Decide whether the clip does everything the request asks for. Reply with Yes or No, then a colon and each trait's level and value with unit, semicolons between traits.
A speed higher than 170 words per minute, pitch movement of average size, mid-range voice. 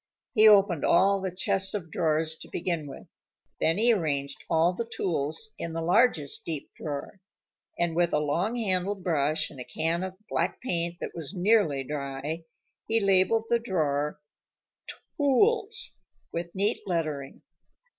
No: average, 150 wpm; average, 4.7 semitones; medium, 170 Hz